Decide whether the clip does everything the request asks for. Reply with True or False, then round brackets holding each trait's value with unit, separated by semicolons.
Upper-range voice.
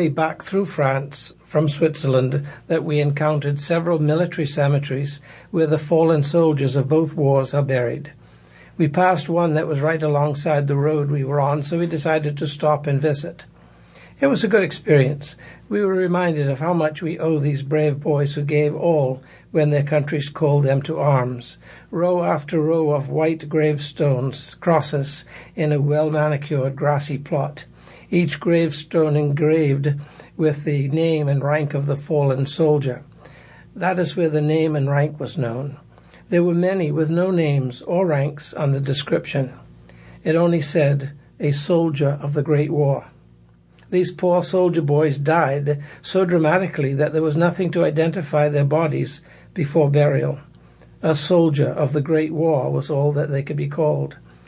False (150 Hz)